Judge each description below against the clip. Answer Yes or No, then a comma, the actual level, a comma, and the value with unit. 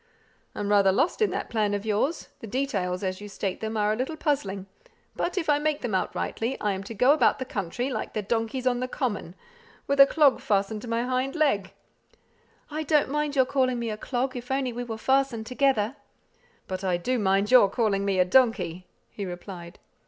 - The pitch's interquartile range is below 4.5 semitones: No, average, 5.0 semitones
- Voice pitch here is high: Yes, high, 230 Hz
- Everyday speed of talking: No, fast, 210 wpm